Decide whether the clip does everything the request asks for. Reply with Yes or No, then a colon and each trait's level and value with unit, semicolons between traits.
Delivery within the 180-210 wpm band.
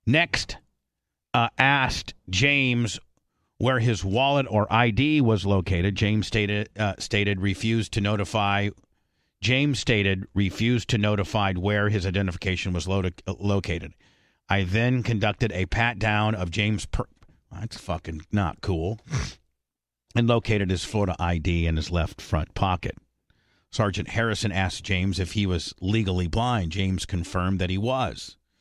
No: average, 140 wpm